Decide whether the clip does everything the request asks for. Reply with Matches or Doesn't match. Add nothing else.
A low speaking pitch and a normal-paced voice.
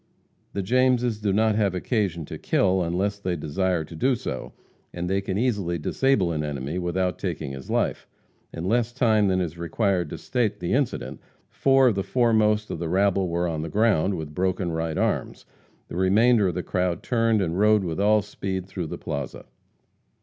Matches